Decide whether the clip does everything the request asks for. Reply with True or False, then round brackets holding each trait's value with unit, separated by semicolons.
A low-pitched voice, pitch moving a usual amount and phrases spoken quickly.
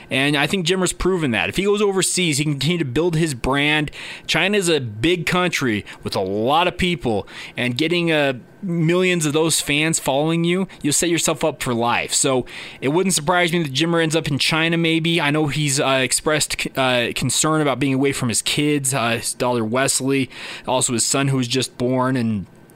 False (150 Hz; 4.3 semitones; 210 wpm)